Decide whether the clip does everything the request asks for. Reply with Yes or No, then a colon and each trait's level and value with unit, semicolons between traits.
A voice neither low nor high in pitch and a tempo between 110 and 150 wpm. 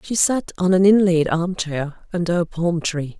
No: medium, 175 Hz; average, 190 wpm